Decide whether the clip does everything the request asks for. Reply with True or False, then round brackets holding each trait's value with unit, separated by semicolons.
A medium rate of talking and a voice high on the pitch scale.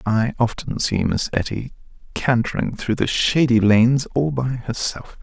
False (150 wpm; 120 Hz)